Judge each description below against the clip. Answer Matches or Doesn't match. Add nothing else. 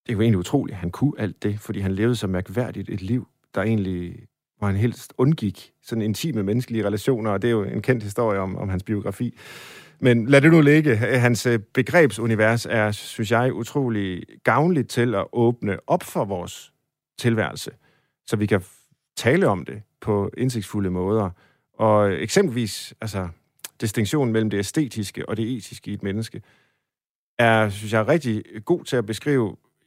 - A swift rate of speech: Doesn't match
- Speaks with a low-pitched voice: Matches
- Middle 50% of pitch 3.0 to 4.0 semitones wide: Matches